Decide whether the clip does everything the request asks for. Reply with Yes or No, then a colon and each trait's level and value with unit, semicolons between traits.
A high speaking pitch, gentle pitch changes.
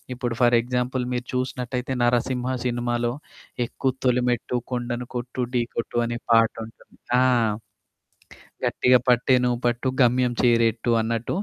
No: low, 120 Hz; narrow, 1.0 semitones